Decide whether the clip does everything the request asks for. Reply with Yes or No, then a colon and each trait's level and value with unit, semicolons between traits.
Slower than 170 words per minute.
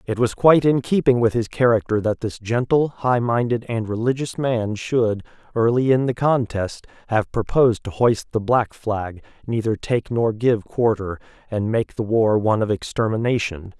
No: average, 175 wpm